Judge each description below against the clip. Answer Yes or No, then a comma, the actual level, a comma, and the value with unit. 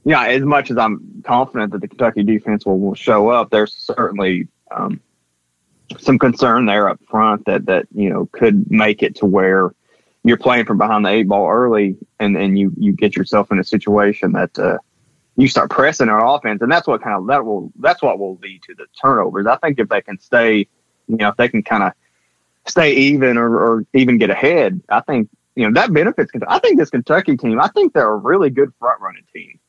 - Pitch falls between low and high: No, low, 105 Hz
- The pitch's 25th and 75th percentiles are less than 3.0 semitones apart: No, average, 3.3 semitones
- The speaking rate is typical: No, fast, 220 wpm